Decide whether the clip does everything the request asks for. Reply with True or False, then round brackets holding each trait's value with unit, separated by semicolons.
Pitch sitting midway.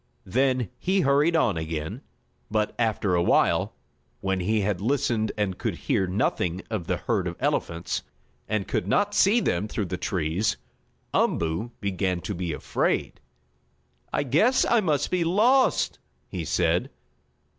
False (105 Hz)